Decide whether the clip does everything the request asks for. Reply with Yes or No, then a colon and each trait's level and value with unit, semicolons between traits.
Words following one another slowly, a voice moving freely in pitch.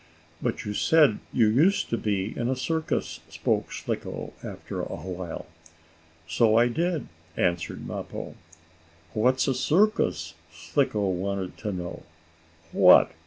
Yes: slow, 125 wpm; wide, 6.3 semitones